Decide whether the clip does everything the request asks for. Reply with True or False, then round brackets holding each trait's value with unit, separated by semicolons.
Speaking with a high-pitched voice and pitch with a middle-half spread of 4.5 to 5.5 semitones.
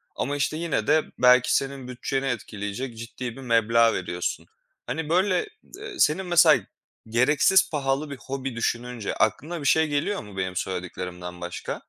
False (130 Hz; 5.2 semitones)